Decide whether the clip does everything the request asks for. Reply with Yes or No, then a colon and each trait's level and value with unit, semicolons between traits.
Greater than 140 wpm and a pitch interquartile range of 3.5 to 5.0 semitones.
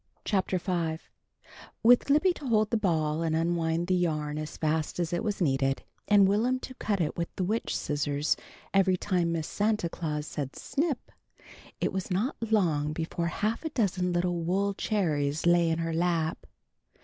Yes: average, 175 wpm; average, 4.2 semitones